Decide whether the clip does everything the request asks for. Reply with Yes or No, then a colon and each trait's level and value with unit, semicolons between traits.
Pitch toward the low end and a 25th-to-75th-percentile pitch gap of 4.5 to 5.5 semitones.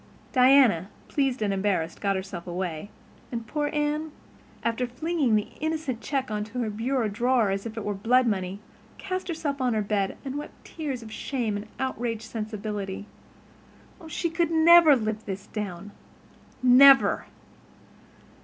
No: high, 230 Hz; average, 5.2 semitones